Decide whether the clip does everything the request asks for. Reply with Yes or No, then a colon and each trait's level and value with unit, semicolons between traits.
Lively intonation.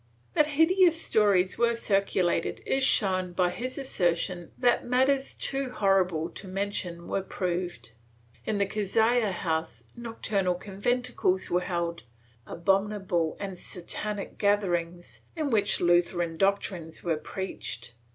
No: average, 4.2 semitones